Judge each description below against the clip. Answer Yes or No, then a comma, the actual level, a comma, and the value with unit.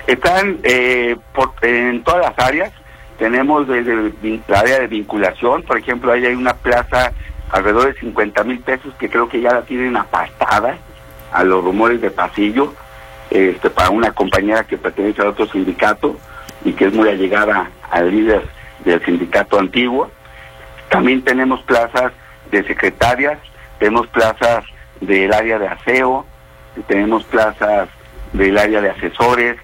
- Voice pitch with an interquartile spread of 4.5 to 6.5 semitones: Yes, average, 5.2 semitones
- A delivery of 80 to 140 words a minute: No, average, 150 wpm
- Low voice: Yes, low, 110 Hz